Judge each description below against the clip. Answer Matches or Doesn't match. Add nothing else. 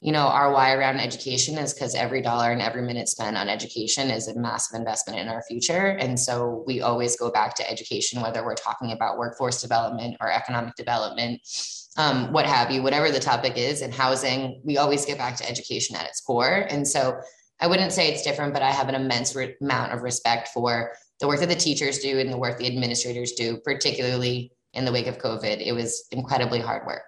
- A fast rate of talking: Matches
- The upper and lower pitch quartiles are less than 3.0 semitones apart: Matches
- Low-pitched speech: Matches